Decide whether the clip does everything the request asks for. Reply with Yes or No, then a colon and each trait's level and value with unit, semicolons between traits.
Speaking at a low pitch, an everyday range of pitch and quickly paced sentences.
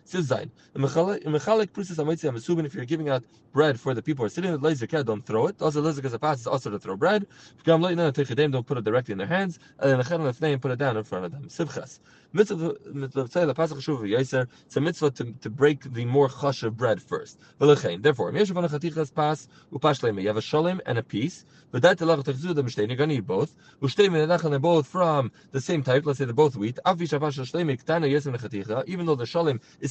No: medium, 150 Hz; average, 3.8 semitones; fast, 235 wpm